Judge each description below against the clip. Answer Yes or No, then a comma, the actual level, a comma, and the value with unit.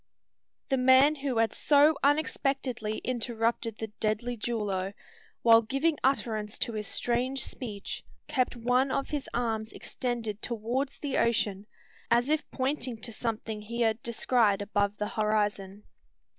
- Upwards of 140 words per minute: No, slow, 135 wpm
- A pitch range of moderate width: Yes, average, 3.3 semitones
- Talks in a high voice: Yes, high, 235 Hz